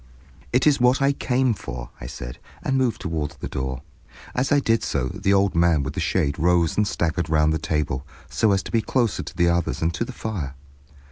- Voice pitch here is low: Yes, very low, 85 Hz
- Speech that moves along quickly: Yes, fast, 220 wpm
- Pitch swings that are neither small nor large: No, wide, 7.6 semitones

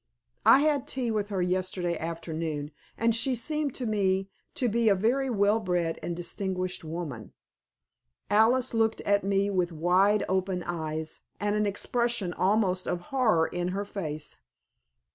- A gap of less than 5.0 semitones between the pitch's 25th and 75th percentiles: Yes, average, 4.1 semitones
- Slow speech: No, average, 150 wpm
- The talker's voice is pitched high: Yes, high, 195 Hz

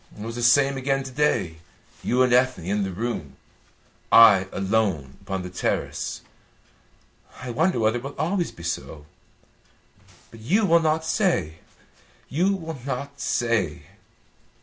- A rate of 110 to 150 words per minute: Yes, average, 145 wpm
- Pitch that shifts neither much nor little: No, wide, 6.7 semitones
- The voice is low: Yes, low, 120 Hz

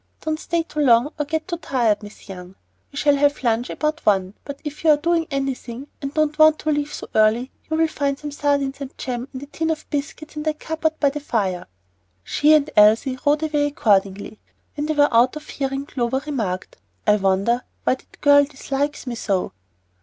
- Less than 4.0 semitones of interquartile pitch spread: No, average, 4.3 semitones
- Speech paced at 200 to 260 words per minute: Yes, fast, 205 wpm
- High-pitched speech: Yes, very high, 280 Hz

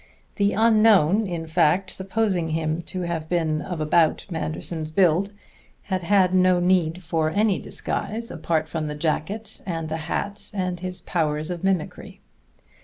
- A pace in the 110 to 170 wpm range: Yes, average, 150 wpm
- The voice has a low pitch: No, medium, 175 Hz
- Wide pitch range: No, average, 3.2 semitones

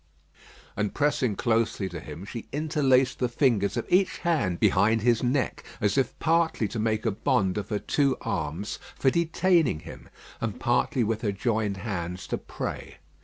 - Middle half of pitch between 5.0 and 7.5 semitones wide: Yes, wide, 5.4 semitones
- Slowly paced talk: No, average, 170 wpm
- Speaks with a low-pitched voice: Yes, low, 115 Hz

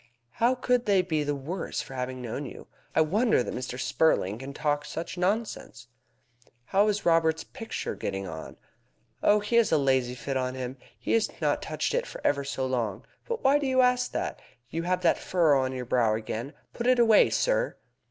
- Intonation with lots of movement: Yes, wide, 8.9 semitones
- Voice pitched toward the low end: No, medium, 160 Hz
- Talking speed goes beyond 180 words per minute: Yes, average, 200 wpm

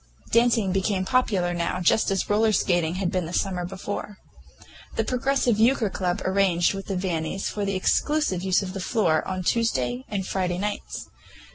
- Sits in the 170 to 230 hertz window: Yes, high, 190 Hz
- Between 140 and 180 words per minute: Yes, average, 170 wpm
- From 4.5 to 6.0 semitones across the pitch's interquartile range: No, average, 2.8 semitones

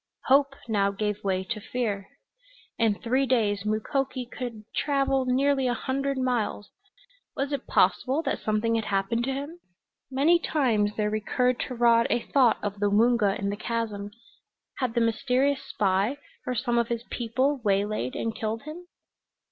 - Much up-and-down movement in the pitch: No, average, 4.0 semitones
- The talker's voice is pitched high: Yes, high, 235 Hz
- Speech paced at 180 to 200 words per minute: No, average, 160 wpm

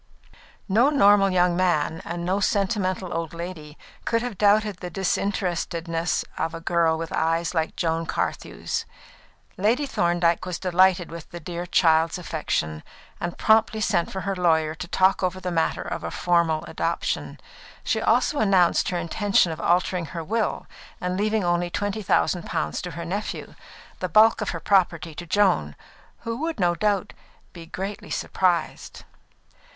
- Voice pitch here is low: No, medium, 180 Hz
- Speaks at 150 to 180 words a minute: Yes, average, 155 wpm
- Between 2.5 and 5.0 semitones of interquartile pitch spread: Yes, average, 2.9 semitones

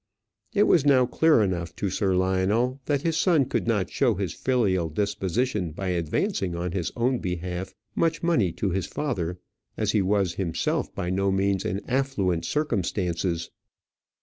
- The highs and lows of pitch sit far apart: Yes, wide, 6.0 semitones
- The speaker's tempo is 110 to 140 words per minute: No, average, 160 wpm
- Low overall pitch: Yes, low, 100 Hz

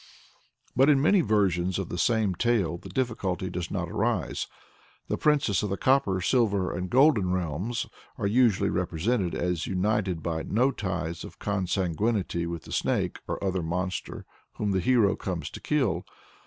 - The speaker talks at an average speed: Yes, average, 160 wpm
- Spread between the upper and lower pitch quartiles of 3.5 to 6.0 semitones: Yes, average, 4.5 semitones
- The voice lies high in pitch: No, very low, 95 Hz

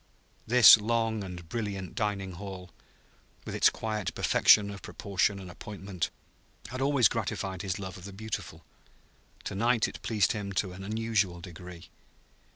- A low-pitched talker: Yes, low, 100 Hz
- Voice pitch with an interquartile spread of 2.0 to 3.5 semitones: Yes, average, 2.7 semitones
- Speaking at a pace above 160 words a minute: No, average, 150 wpm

